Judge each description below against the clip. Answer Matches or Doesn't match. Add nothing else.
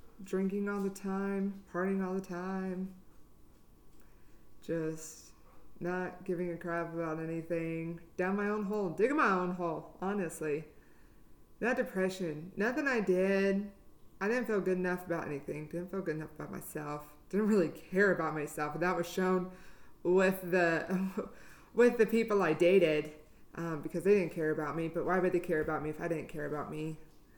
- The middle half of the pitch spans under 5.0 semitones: Matches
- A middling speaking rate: Matches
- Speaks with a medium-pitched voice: Matches